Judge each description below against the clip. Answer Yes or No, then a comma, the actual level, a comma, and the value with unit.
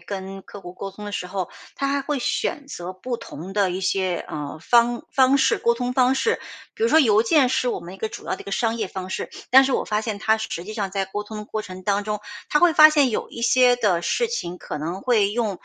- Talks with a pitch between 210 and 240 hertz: Yes, high, 215 Hz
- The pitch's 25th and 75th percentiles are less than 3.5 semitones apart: No, average, 4.8 semitones